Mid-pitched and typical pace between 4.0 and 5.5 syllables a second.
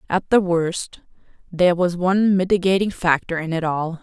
Yes: medium, 175 Hz; 5.1 syllables/s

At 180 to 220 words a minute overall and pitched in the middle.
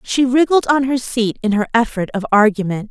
No: fast, 205 wpm; high, 230 Hz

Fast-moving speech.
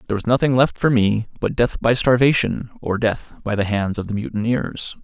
Yes: fast, 215 wpm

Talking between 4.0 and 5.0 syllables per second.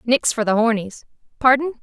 No: 5.5 syllables/s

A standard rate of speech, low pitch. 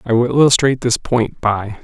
Yes: average, 195 wpm; low, 120 Hz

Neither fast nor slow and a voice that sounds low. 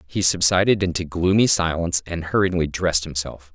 Yes: average, 150 wpm; very low, 85 Hz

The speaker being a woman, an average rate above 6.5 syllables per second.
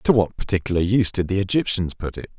No: male; 6.7 syllables/s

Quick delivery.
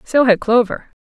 No: average, 175 wpm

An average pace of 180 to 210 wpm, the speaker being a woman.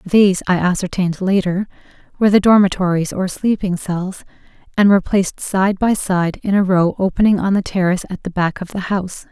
Yes: average, 185 wpm; female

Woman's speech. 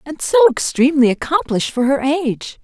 Yes: female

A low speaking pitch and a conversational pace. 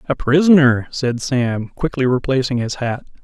Yes: low, 130 Hz; average, 150 wpm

